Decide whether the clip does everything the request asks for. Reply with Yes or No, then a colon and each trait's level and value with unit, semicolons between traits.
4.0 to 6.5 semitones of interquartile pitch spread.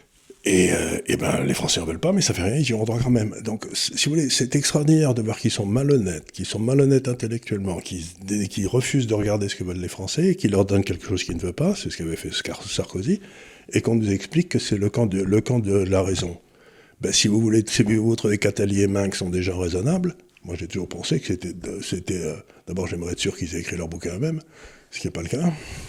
Yes: average, 4.9 semitones